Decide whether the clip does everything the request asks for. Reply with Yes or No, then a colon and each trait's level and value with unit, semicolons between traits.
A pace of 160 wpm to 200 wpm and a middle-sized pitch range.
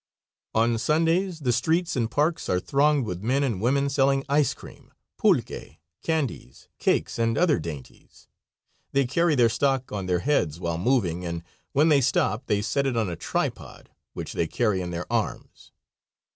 No: average, 170 wpm; wide, 7.3 semitones